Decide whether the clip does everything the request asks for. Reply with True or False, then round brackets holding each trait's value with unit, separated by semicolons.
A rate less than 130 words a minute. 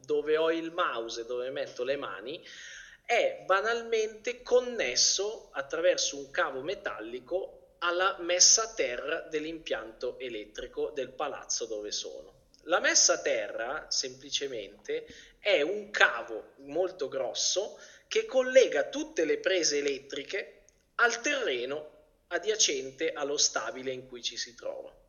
True (120 wpm)